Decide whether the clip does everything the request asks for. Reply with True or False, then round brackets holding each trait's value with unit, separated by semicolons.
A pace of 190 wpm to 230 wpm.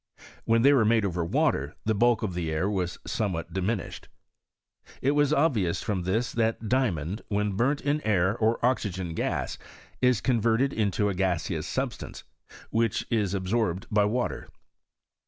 False (155 wpm)